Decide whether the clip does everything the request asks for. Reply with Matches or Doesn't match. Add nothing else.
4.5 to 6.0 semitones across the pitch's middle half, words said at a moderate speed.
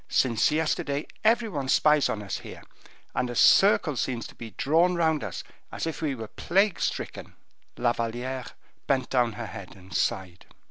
Matches